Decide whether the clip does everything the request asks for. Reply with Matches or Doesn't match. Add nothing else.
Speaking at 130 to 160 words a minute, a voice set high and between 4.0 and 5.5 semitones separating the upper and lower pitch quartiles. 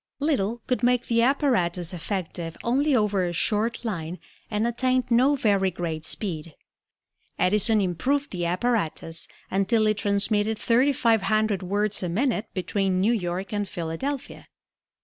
Matches